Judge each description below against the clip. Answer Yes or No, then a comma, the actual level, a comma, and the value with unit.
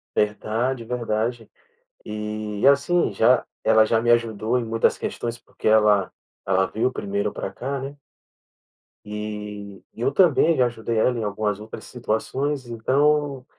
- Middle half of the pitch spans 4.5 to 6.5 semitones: No, average, 3.2 semitones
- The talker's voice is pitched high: No, low, 115 Hz